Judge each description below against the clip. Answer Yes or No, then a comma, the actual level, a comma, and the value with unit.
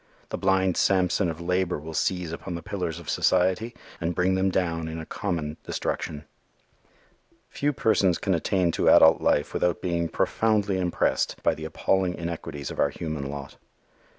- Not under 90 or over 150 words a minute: No, average, 165 wpm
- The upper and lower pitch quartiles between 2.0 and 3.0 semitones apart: Yes, narrow, 2.6 semitones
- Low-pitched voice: Yes, very low, 90 Hz